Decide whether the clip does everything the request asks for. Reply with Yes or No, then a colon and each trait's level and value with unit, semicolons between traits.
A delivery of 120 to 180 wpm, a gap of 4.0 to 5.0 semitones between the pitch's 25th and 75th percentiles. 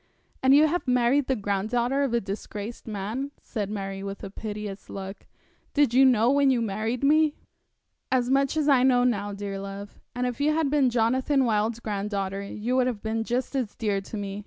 No: average, 195 wpm; average, 4.5 semitones